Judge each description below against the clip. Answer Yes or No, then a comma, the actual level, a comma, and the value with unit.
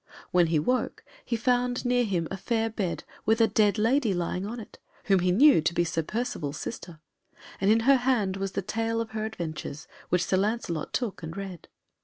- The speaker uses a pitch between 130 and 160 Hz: No, high, 205 Hz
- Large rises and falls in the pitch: No, average, 4.6 semitones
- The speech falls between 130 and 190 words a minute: No, fast, 205 wpm